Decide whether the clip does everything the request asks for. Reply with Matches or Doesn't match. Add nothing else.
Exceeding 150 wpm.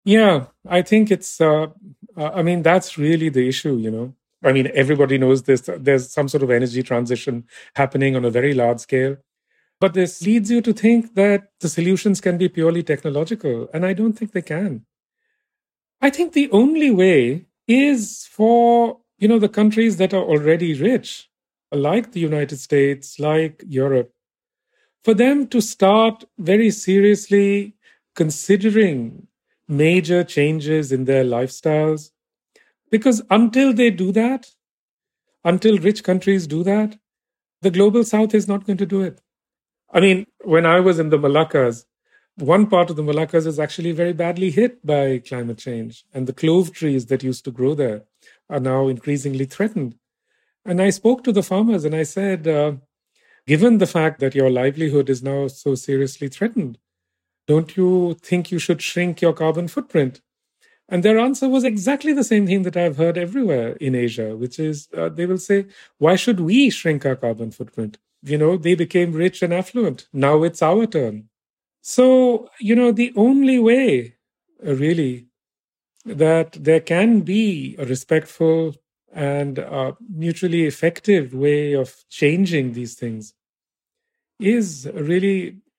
Matches